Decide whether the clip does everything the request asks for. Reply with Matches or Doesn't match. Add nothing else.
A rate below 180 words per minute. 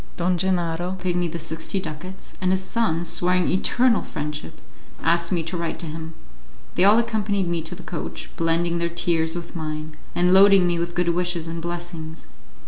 Doesn't match